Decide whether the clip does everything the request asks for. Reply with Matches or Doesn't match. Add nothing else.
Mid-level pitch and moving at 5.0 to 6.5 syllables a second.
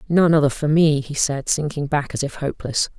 Matches